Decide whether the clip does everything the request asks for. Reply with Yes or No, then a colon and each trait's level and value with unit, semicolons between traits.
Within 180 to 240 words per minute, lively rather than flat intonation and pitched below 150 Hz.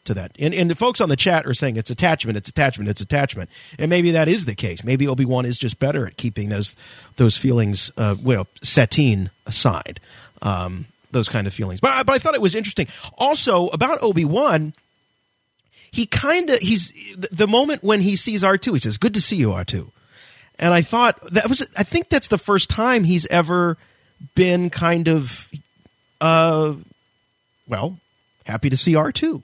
No: average, 185 wpm; wide, 8.9 semitones; medium, 155 Hz